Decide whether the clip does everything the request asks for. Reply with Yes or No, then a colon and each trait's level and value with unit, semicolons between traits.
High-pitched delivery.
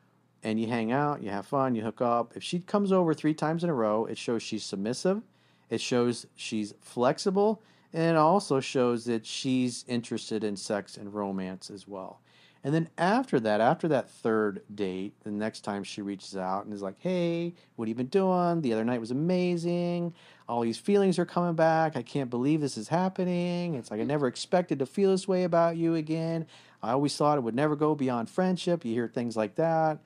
No: low, 135 Hz